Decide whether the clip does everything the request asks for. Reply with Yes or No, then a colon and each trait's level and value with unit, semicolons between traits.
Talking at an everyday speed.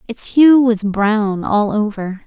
Yes: average, 160 wpm